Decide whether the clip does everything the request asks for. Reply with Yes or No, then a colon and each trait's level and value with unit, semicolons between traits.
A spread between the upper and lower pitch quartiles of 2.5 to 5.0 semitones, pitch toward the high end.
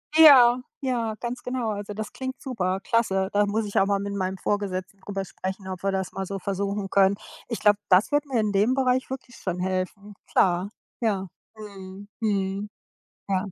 Yes: average, 3.1 semitones; high, 200 Hz